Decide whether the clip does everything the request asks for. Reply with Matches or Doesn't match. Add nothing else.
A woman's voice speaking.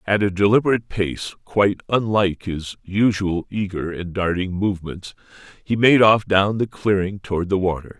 Doesn't match